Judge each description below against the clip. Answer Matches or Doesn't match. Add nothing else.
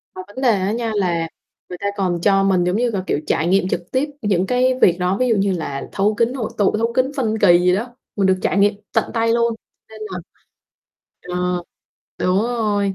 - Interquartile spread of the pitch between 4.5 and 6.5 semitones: Doesn't match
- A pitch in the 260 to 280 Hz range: Doesn't match